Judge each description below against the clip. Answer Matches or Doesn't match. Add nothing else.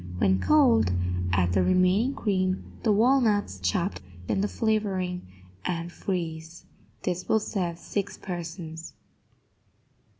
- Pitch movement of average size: Matches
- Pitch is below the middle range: Doesn't match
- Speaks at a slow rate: Matches